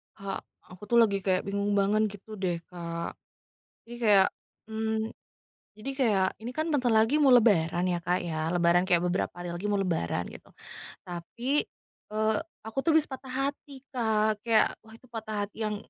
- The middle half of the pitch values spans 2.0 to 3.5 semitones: No, average, 4.1 semitones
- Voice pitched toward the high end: Yes, high, 210 Hz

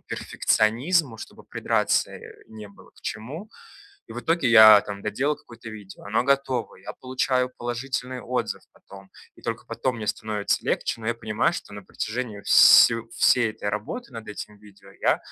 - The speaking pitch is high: No, low, 115 Hz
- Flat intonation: No, average, 3.2 semitones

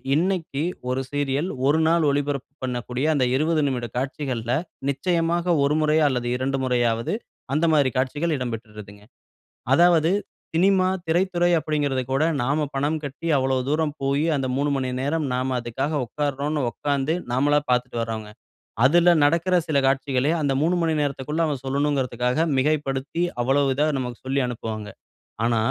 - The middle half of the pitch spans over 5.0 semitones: No, average, 3.3 semitones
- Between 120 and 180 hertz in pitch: Yes, medium, 140 Hz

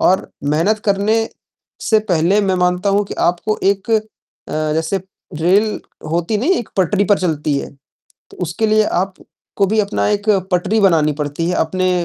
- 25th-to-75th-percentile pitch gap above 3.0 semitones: Yes, average, 3.7 semitones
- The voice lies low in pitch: No, high, 190 Hz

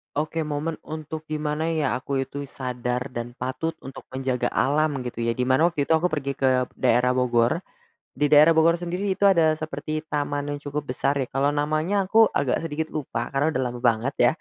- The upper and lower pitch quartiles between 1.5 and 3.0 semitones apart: No, average, 3.4 semitones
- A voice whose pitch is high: No, medium, 145 Hz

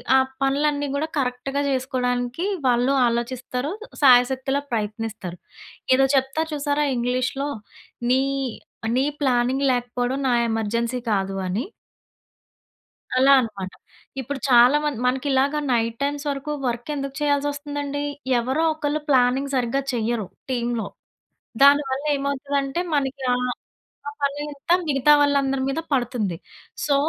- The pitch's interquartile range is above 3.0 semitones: No, average, 2.7 semitones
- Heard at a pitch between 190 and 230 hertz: No, very high, 265 Hz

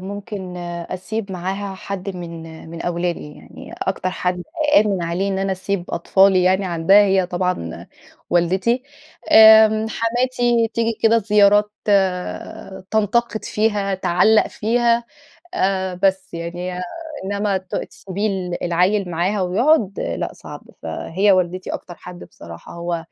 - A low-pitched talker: No, high, 190 Hz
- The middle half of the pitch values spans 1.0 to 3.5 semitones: Yes, average, 2.8 semitones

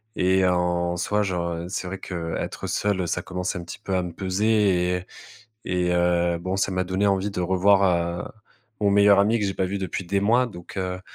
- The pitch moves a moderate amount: No, narrow, 2.0 semitones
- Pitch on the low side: Yes, very low, 95 Hz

